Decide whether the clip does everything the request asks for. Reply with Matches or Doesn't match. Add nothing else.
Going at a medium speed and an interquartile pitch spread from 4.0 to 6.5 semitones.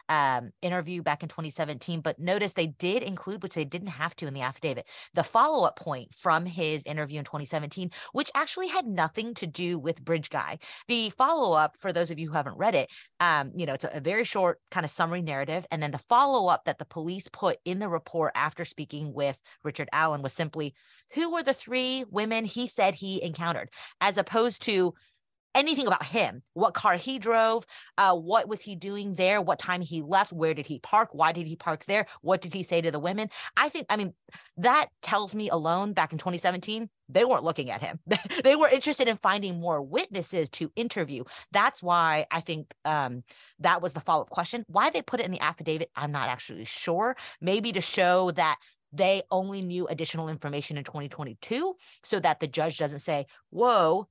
Doesn't match